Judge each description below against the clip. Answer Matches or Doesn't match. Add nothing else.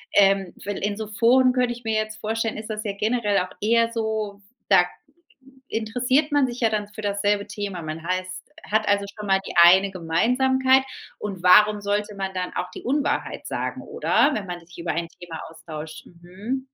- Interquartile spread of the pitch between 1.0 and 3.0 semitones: Doesn't match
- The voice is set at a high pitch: Matches